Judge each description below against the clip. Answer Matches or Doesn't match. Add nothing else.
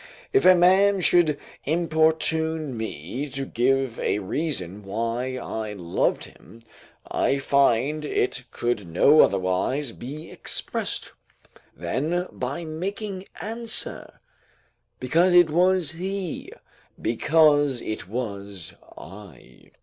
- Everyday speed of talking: Doesn't match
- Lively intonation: Matches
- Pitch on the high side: Doesn't match